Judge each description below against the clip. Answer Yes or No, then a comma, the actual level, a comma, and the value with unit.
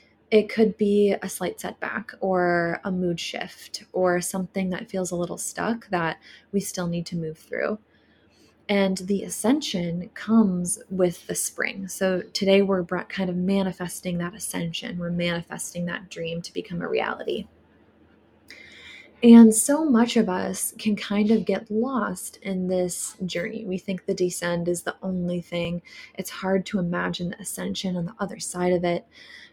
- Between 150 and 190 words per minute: Yes, average, 165 wpm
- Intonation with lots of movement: No, narrow, 2.5 semitones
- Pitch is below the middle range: No, high, 190 Hz